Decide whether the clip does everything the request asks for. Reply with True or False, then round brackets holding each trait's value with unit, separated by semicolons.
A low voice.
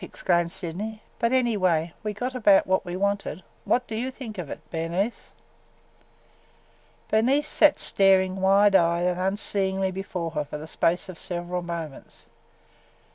False (190 Hz)